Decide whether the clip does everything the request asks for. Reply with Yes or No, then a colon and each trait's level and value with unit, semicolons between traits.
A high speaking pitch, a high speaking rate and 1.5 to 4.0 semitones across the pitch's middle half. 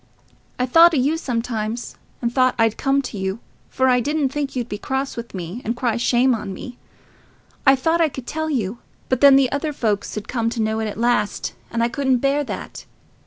Yes: very high, 250 Hz; fast, 215 wpm; average, 3.3 semitones